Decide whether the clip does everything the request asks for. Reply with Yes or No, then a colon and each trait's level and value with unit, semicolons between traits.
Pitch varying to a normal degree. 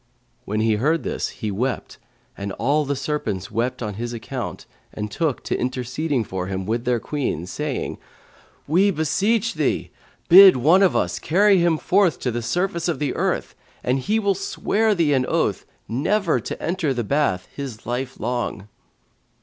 No: wide, 6.7 semitones